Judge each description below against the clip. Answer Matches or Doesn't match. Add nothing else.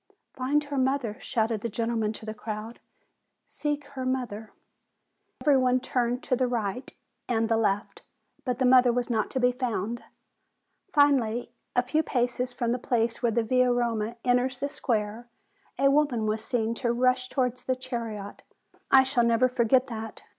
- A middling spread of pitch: Doesn't match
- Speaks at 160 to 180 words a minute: Matches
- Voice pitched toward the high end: Matches